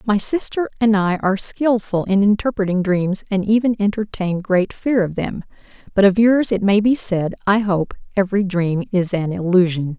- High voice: Yes, high, 200 Hz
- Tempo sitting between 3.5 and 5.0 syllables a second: Yes, 4.9 syllables/s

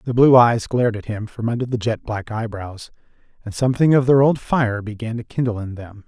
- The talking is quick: Yes, fast, 225 wpm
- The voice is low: Yes, low, 115 Hz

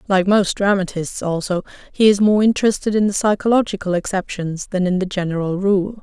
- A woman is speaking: Yes, female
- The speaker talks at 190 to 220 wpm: No, average, 170 wpm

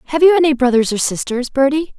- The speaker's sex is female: Yes, female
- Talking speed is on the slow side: No, fast, 210 wpm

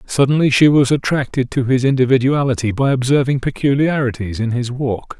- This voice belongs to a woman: No, male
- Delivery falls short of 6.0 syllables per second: Yes, 5.5 syllables/s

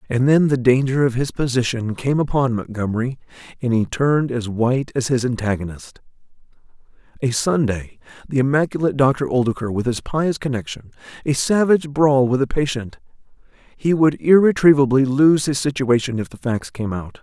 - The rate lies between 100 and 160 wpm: Yes, average, 155 wpm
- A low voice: Yes, low, 130 Hz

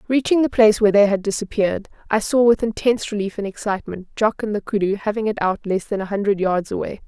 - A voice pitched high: Yes, high, 210 Hz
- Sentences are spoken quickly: Yes, fast, 230 wpm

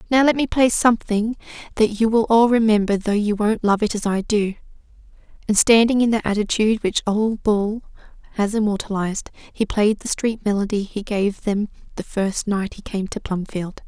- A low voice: No, high, 210 Hz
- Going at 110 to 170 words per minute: No, average, 185 wpm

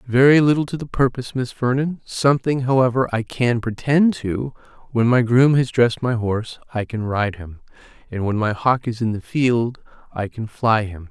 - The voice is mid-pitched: No, low, 120 Hz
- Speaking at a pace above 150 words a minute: Yes, average, 190 wpm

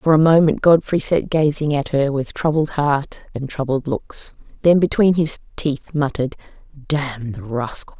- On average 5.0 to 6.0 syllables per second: No, 4.4 syllables/s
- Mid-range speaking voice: Yes, medium, 145 Hz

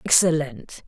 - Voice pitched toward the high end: No, medium, 150 Hz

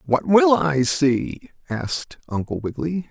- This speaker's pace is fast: No, slow, 135 wpm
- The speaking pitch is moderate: Yes, medium, 150 Hz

